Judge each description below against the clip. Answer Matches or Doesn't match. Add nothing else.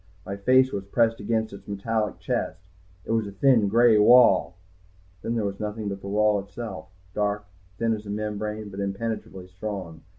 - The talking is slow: Doesn't match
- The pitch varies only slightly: Matches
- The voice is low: Matches